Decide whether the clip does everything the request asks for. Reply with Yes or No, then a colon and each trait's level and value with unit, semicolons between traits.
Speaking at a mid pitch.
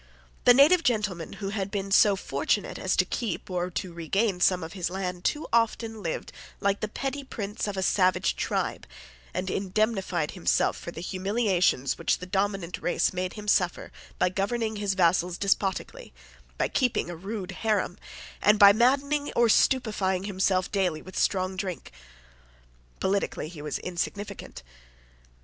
No: high, 195 Hz